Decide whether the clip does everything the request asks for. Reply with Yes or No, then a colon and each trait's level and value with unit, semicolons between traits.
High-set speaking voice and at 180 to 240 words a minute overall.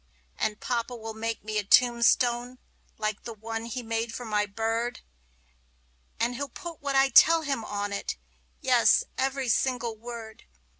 No: high, 235 Hz; average, 155 wpm